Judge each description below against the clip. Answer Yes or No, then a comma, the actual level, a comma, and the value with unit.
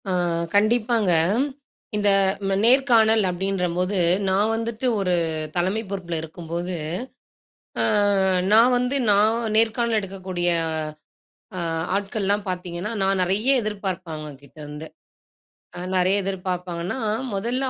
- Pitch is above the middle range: Yes, high, 195 Hz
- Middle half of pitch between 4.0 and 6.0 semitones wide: No, average, 3.5 semitones